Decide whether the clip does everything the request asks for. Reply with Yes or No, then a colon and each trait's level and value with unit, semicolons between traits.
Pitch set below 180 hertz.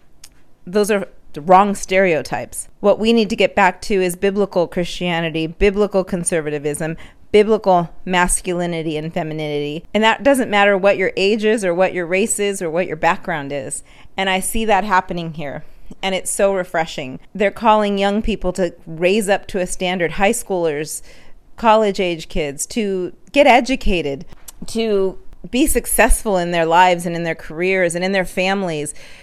No: medium, 185 Hz